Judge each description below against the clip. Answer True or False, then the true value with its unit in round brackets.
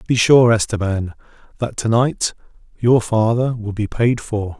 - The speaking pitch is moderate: False (110 Hz)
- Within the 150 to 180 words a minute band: True (155 wpm)